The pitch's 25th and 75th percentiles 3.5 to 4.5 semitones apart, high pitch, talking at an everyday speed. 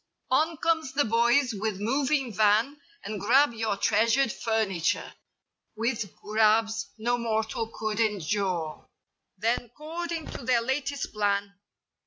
No: average, 3.9 semitones; high, 225 Hz; slow, 120 wpm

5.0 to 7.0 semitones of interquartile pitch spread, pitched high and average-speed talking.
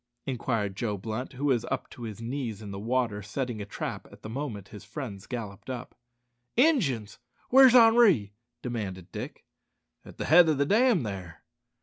No: wide, 5.6 semitones; low, 120 Hz; average, 175 wpm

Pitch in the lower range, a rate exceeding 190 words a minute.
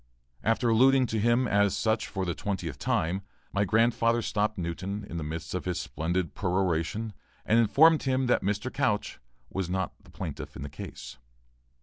No: low, 100 Hz; average, 175 wpm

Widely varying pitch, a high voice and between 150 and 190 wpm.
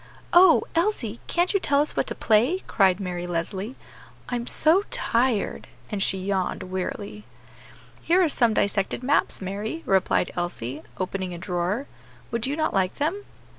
Yes: wide, 7.4 semitones; high, 210 Hz; average, 155 wpm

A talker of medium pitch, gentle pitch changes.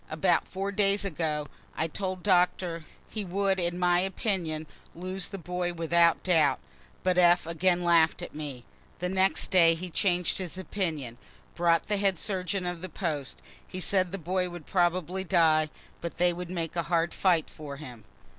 Yes: medium, 175 Hz; narrow, 2.1 semitones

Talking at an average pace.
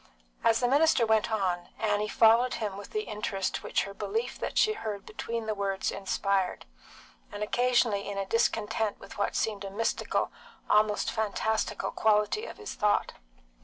Yes: average, 165 wpm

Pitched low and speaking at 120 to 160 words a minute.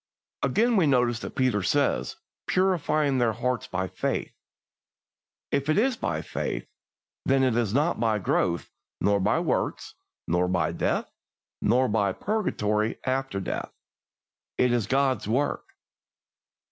Yes: low, 125 Hz; slow, 135 wpm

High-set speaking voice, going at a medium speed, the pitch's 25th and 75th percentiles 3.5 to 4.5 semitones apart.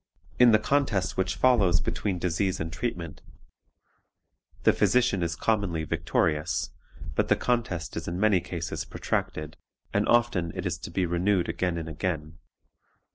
No: very low, 90 Hz; average, 150 wpm; average, 4.0 semitones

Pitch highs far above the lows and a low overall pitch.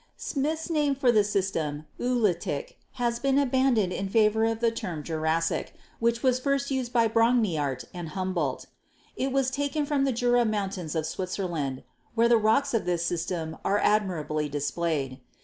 No: wide, 7.1 semitones; high, 215 Hz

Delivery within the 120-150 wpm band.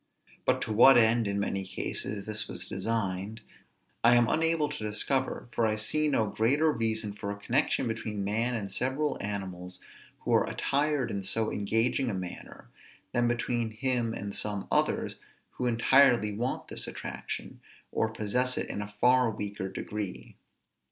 No: average, 160 wpm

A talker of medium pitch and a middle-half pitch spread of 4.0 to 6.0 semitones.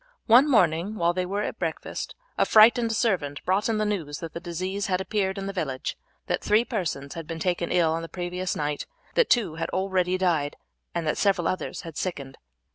No: medium, 180 Hz; average, 3.6 semitones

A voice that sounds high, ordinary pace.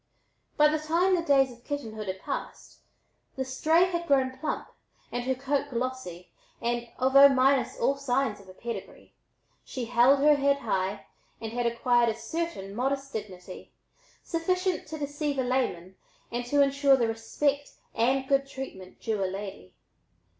Yes: very high, 260 Hz; average, 155 wpm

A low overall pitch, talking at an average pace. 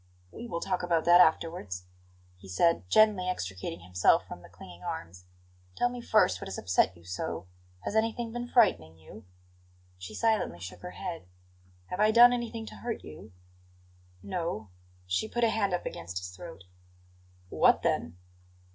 No: medium, 165 Hz; average, 165 wpm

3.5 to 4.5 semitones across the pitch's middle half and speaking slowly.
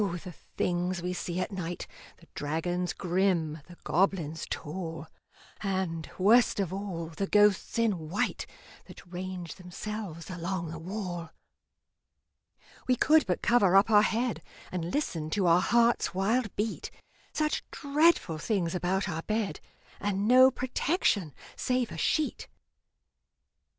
Yes: average, 3.9 semitones; slow, 130 wpm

